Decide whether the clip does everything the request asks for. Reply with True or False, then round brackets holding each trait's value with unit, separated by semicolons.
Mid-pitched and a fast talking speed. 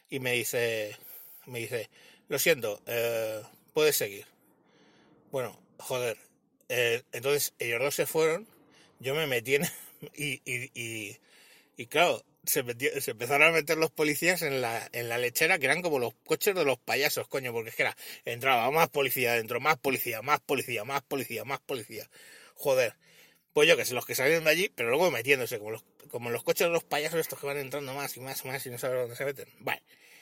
True (160 Hz; 205 wpm)